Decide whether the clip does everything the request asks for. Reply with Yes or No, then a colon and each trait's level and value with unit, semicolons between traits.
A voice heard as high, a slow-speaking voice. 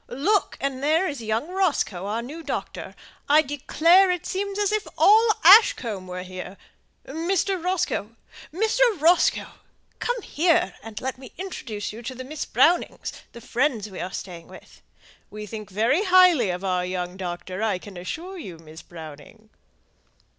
No: very high, 260 Hz; average, 155 wpm